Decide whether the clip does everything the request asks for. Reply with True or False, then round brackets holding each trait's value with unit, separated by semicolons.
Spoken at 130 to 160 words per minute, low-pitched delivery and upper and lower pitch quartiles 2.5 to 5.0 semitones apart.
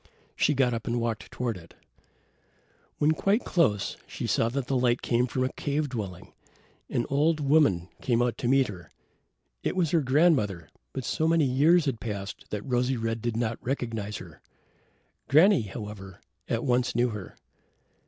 False (170 wpm; 120 Hz; 4.5 semitones)